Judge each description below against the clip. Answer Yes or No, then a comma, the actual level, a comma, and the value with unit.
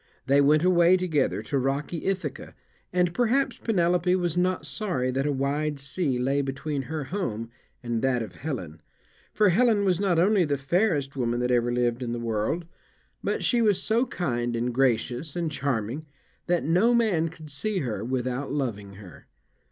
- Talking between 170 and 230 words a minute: Yes, average, 175 wpm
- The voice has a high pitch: No, medium, 145 Hz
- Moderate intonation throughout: No, wide, 6.3 semitones